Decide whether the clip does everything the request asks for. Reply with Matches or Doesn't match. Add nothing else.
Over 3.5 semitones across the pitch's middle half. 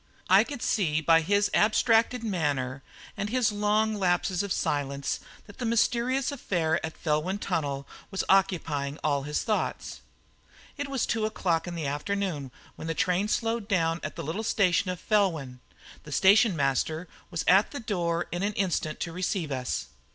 Matches